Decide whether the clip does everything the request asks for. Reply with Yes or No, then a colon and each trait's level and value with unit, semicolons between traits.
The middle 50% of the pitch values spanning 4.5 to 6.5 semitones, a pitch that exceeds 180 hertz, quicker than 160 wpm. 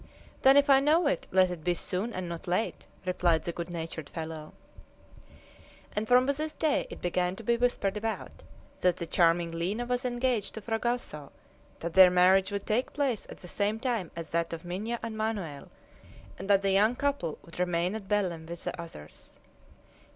Yes: wide, 5.5 semitones; high, 190 Hz; average, 190 wpm